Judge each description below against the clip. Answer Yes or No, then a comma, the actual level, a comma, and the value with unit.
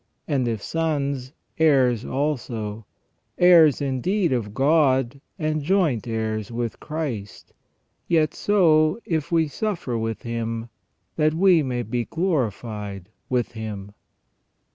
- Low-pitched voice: Yes, low, 130 Hz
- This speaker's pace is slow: Yes, slow, 120 wpm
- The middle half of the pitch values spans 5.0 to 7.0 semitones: Yes, wide, 5.6 semitones